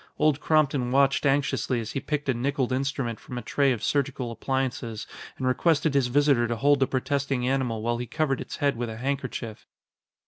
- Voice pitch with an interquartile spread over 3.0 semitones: No, narrow, 2.6 semitones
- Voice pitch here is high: No, low, 135 Hz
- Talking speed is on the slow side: No, average, 195 wpm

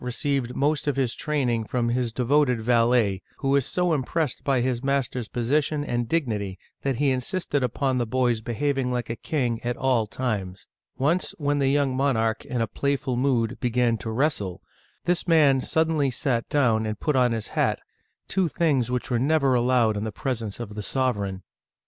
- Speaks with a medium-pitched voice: No, low, 125 Hz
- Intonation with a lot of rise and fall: No, average, 3.4 semitones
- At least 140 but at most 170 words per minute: No, average, 180 wpm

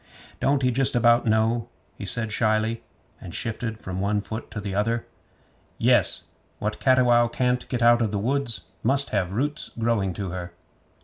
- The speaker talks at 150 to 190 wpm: Yes, average, 165 wpm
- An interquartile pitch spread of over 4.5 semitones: No, narrow, 2.6 semitones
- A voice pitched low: Yes, low, 115 Hz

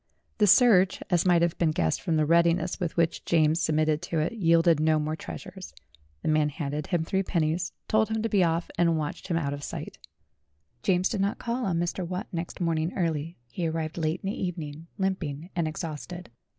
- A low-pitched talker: No, medium, 170 Hz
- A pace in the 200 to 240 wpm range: Yes, fast, 205 wpm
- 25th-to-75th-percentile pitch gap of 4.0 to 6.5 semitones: No, average, 2.7 semitones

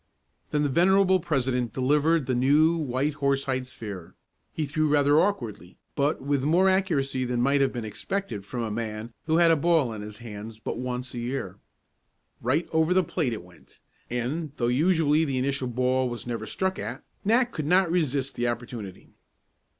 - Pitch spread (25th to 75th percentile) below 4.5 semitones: No, average, 4.9 semitones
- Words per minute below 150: No, average, 180 wpm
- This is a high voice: No, low, 135 Hz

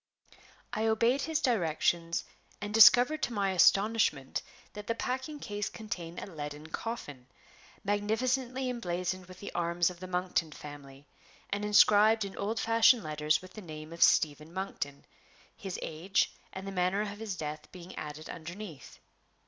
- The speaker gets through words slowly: No, average, 150 wpm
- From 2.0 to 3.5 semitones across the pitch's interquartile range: No, average, 5.3 semitones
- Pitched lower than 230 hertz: Yes, high, 190 Hz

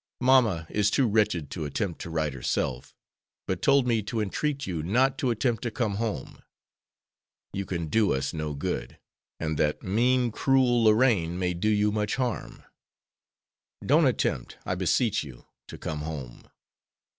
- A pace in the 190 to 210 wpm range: No, average, 155 wpm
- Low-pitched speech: Yes, low, 105 Hz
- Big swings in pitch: Yes, wide, 6.7 semitones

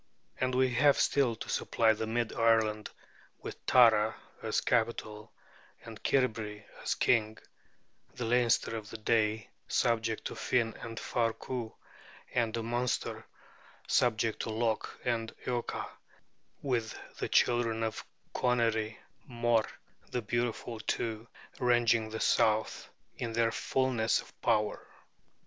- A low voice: Yes, low, 115 Hz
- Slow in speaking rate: Yes, slow, 125 wpm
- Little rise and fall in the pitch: Yes, narrow, 1.5 semitones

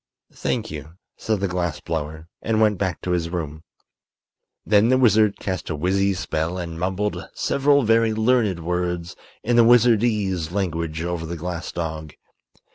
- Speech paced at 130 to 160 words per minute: Yes, average, 155 wpm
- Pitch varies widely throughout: No, average, 4.5 semitones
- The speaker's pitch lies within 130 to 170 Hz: No, very low, 90 Hz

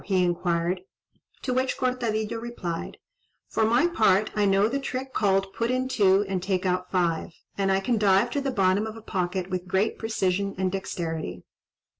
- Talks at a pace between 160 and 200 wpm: Yes, average, 180 wpm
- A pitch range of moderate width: Yes, average, 3.6 semitones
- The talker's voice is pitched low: No, high, 195 Hz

